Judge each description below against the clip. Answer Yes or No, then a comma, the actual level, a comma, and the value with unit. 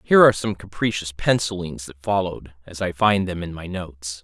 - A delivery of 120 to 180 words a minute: No, average, 200 wpm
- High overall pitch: No, very low, 90 Hz